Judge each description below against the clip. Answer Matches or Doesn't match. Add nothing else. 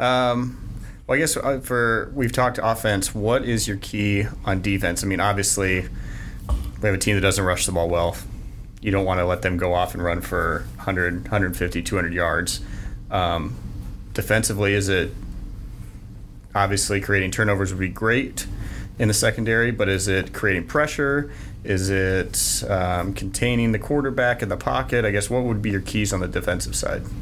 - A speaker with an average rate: Matches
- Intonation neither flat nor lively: Matches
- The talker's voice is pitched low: Matches